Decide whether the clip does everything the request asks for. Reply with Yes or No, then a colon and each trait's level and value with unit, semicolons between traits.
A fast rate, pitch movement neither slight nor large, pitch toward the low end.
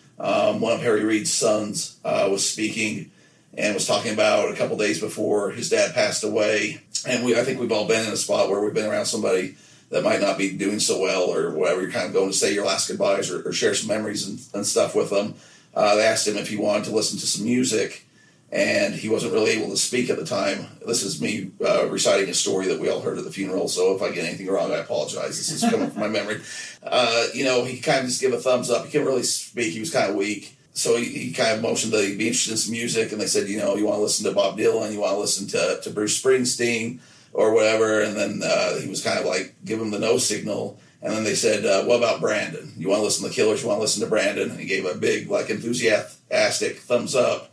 Yes: fast, 270 wpm; average, 3.7 semitones; low, 110 Hz